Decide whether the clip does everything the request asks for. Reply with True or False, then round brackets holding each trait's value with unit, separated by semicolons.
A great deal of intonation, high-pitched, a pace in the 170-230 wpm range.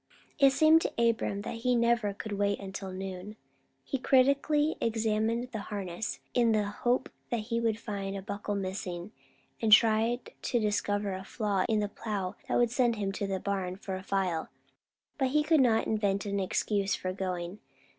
False (3.2 semitones; 210 Hz; 180 wpm)